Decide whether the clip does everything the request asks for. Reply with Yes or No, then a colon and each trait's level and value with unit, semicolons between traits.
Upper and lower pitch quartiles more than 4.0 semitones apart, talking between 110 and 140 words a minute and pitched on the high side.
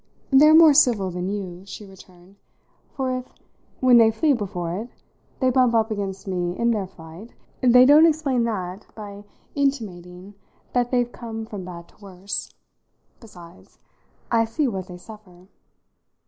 No: average, 5.1 semitones; average, 150 wpm; high, 210 Hz